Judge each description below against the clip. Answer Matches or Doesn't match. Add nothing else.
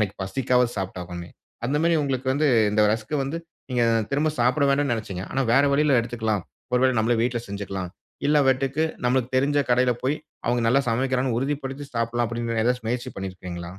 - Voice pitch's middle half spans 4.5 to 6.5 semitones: Doesn't match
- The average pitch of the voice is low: Matches